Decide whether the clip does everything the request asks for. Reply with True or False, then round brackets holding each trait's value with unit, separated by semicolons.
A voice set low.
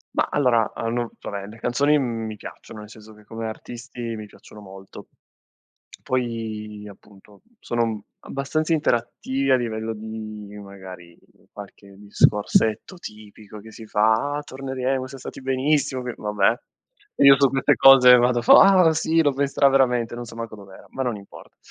True (115 Hz)